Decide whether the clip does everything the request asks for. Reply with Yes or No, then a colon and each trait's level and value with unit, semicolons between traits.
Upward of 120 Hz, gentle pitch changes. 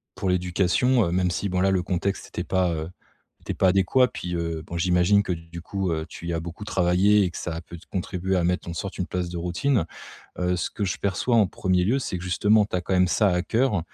No: very low, 90 Hz; narrow, 2.2 semitones